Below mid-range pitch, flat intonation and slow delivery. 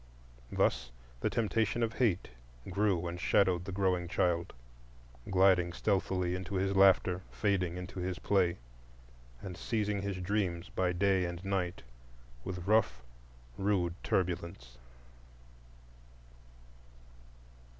Yes: very low, 90 Hz; narrow, 2.1 semitones; slow, 105 wpm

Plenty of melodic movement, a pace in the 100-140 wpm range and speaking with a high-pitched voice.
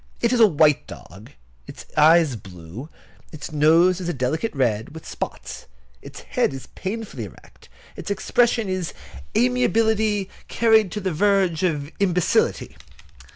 No: wide, 6.7 semitones; slow, 135 wpm; medium, 170 Hz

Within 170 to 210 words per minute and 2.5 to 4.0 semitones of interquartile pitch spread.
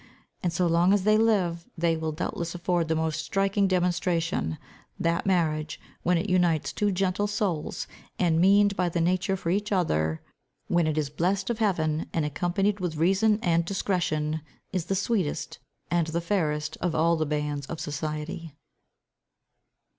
No: average, 160 wpm; average, 3.2 semitones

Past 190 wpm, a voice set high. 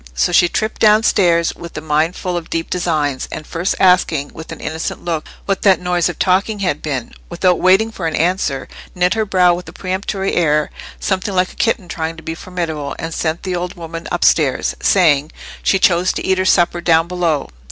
No: fast, 205 wpm; medium, 175 Hz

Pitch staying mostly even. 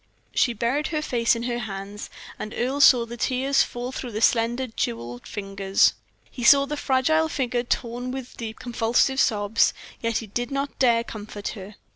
No: average, 3.2 semitones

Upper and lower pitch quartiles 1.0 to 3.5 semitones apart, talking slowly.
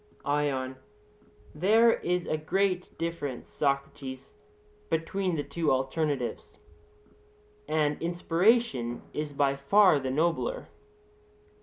No: average, 4.3 semitones; slow, 95 wpm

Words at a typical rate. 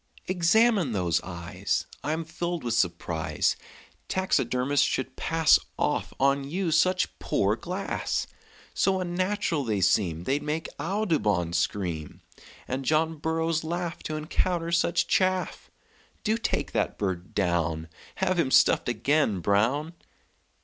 No: slow, 120 wpm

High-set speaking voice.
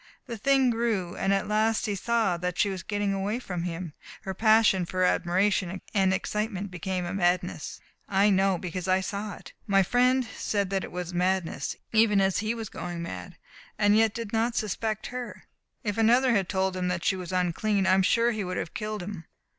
Yes: high, 195 Hz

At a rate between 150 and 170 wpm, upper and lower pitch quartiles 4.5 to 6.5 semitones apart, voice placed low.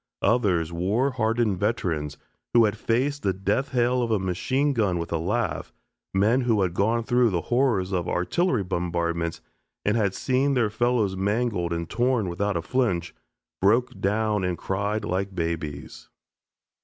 Yes: average, 155 wpm; average, 5.1 semitones; low, 105 Hz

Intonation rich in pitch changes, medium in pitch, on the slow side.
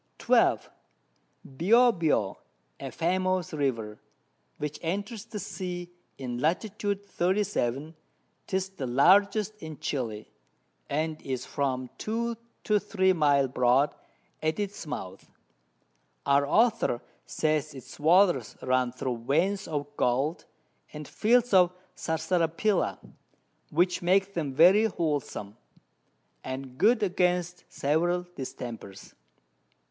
Yes: wide, 5.7 semitones; medium, 165 Hz; slow, 105 wpm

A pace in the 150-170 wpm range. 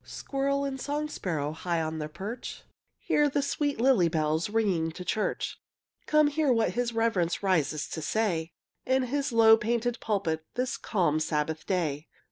Yes: average, 160 wpm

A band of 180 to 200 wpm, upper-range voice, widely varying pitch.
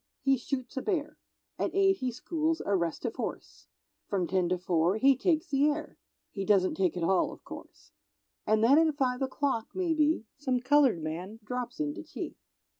Yes: average, 185 wpm; very high, 250 Hz; wide, 7.6 semitones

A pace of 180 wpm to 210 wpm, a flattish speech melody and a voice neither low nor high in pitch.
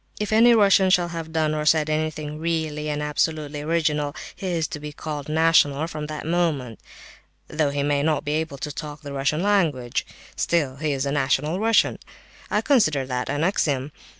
Yes: average, 185 wpm; narrow, 2.2 semitones; medium, 155 Hz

